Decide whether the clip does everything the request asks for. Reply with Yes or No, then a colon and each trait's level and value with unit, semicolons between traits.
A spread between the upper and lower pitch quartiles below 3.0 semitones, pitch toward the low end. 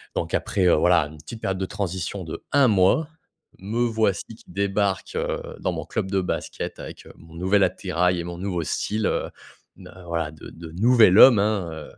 No: average, 3.3 semitones; very low, 95 Hz